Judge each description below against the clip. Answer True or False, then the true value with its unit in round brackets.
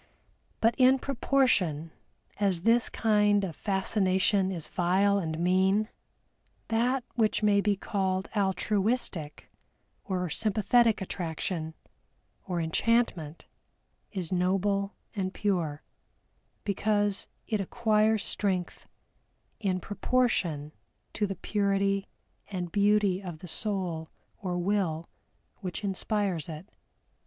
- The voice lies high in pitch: True (195 Hz)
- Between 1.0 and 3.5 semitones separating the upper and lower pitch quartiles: True (2.8 semitones)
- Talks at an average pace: False (100 wpm)